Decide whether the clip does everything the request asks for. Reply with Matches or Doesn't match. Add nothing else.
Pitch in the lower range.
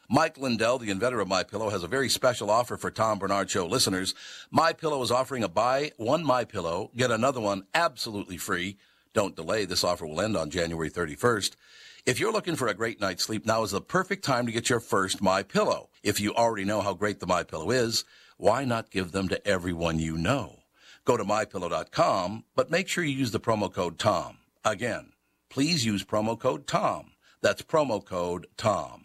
Matches